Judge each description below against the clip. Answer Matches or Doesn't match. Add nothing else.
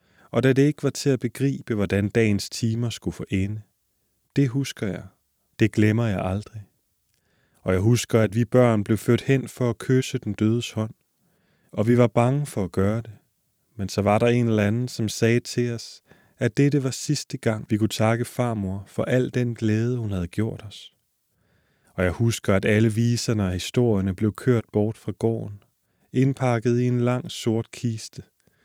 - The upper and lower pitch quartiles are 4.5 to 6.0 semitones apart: Doesn't match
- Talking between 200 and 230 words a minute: Doesn't match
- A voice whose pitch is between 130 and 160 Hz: Doesn't match